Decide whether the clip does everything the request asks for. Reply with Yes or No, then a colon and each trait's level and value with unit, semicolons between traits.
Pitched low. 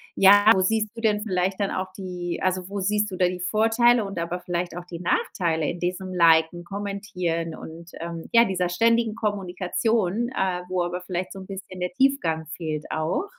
No: medium, 185 Hz